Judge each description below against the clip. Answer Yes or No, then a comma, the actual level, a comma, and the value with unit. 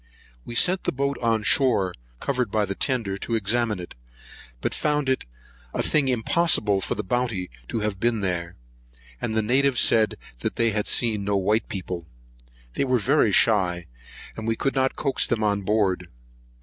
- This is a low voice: Yes, low, 110 Hz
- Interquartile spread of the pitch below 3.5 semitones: No, average, 4.3 semitones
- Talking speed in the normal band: Yes, average, 175 wpm